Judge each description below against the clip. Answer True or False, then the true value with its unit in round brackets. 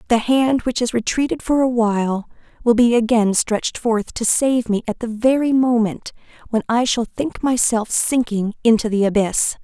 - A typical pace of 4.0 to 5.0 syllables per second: True (4.7 syllables/s)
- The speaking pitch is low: False (230 Hz)